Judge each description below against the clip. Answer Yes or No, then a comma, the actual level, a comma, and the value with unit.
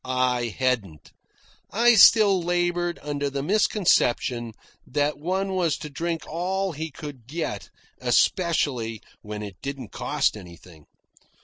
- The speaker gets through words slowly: Yes, slow, 120 wpm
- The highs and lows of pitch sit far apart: Yes, wide, 6.4 semitones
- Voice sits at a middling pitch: Yes, medium, 145 Hz